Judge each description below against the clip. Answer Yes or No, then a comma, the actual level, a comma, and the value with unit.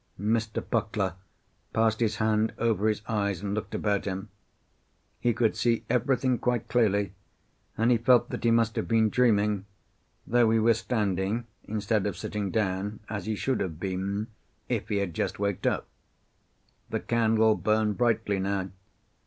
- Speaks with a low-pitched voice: Yes, low, 110 Hz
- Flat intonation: Yes, narrow, 2.2 semitones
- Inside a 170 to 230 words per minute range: No, average, 160 wpm